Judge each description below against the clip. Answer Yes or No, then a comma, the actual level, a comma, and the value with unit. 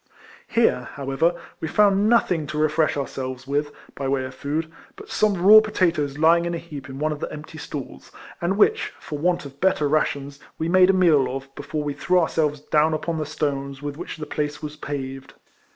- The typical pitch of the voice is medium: Yes, medium, 150 Hz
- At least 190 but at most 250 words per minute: Yes, average, 200 wpm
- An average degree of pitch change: Yes, average, 3.5 semitones